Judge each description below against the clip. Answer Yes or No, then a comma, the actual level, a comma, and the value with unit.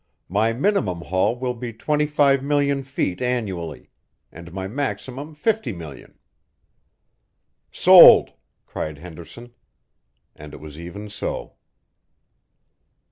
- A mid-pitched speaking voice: No, low, 115 Hz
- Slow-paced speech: Yes, slow, 110 wpm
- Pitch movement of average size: No, wide, 8.1 semitones